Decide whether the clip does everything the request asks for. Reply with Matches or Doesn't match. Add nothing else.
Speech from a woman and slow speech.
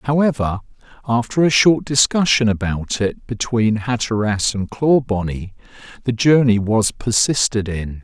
Doesn't match